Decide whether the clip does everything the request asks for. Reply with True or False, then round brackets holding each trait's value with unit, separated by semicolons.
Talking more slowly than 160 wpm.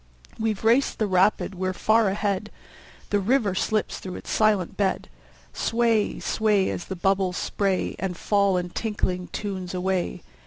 True (150 wpm)